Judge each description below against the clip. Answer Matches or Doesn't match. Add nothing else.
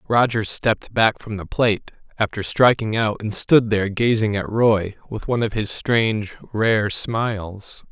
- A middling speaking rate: Matches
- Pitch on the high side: Doesn't match